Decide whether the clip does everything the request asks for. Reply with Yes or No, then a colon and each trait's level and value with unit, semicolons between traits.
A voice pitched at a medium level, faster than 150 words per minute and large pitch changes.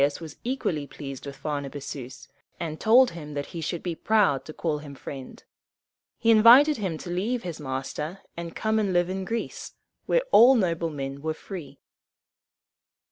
Yes: medium, 165 Hz; average, 170 wpm; wide, 6.8 semitones